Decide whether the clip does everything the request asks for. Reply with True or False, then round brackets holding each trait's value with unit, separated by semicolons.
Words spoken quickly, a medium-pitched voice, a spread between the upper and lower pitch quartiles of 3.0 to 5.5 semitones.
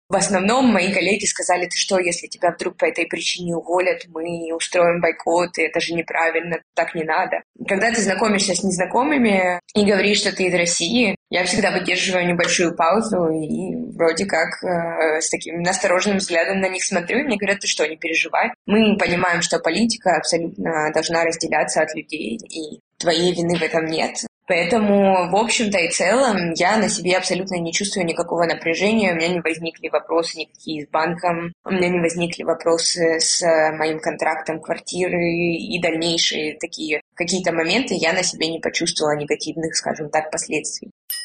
False (170 wpm; 175 Hz; 2.4 semitones)